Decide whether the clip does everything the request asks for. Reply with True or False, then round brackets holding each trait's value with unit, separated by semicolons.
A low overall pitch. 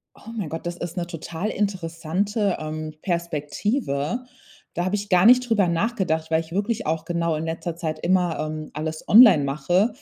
False (170 Hz)